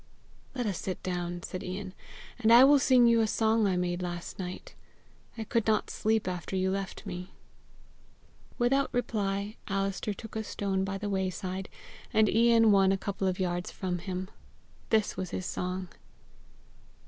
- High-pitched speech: Yes, high, 195 Hz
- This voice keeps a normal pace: Yes, average, 165 wpm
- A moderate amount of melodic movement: Yes, average, 3.0 semitones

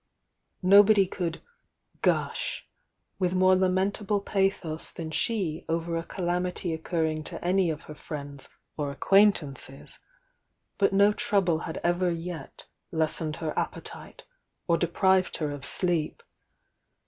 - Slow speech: Yes, slow, 125 wpm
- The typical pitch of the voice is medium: Yes, medium, 175 Hz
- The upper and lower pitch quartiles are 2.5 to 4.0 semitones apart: Yes, average, 3.1 semitones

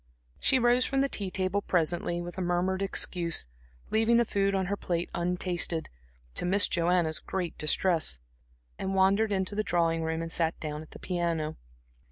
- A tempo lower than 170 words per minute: No, average, 175 wpm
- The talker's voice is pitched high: No, medium, 180 Hz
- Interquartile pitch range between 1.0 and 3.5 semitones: Yes, average, 2.8 semitones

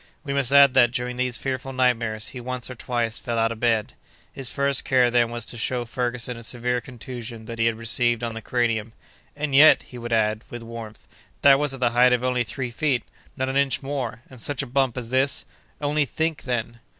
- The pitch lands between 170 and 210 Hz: No, low, 125 Hz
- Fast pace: Yes, fast, 215 wpm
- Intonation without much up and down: Yes, narrow, 2.2 semitones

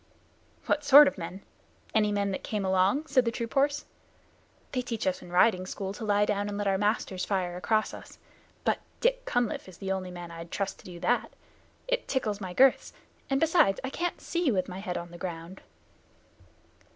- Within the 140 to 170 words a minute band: No, average, 200 wpm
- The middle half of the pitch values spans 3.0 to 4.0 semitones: No, average, 5.3 semitones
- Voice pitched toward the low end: No, high, 205 Hz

